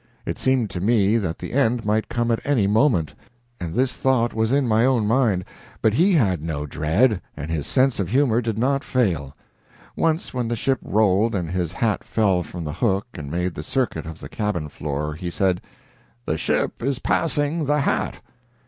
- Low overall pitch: Yes, low, 110 Hz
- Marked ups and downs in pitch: Yes, wide, 6.4 semitones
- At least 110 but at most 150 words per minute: No, average, 195 wpm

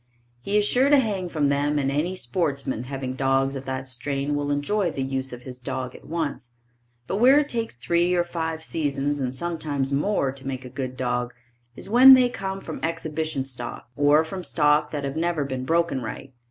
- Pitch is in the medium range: Yes, medium, 145 Hz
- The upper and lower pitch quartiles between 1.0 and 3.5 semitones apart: No, average, 4.4 semitones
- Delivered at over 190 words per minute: Yes, fast, 205 wpm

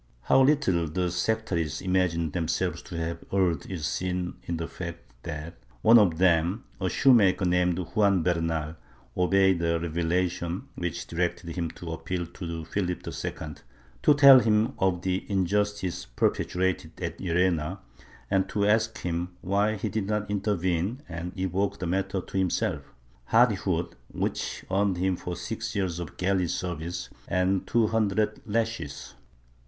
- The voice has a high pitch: No, very low, 90 Hz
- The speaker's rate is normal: Yes, average, 150 wpm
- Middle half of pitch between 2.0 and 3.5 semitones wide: Yes, average, 3.0 semitones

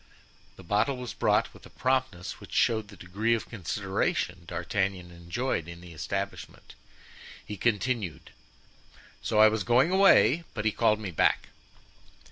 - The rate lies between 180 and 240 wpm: No, average, 145 wpm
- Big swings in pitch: No, average, 4.7 semitones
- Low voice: Yes, low, 105 Hz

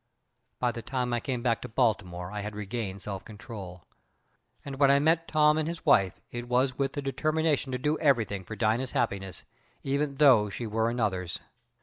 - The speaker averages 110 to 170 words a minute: No, average, 190 wpm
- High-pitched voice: No, low, 120 Hz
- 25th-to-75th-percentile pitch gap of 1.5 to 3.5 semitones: No, average, 4.9 semitones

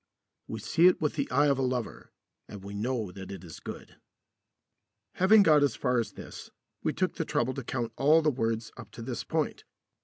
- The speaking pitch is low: Yes, low, 125 Hz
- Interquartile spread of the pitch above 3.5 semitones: Yes, average, 4.6 semitones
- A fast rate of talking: Yes, fast, 210 wpm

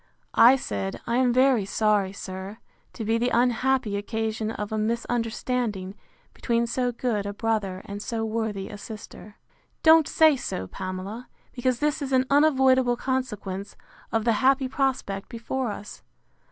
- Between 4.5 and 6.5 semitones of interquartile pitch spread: No, average, 3.9 semitones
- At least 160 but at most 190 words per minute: No, average, 150 wpm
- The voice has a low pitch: No, high, 230 Hz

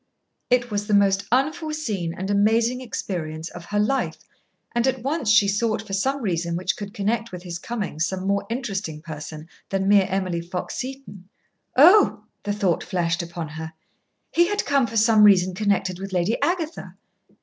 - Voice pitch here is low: No, high, 200 Hz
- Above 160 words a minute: Yes, average, 170 wpm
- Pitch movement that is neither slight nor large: Yes, average, 4.9 semitones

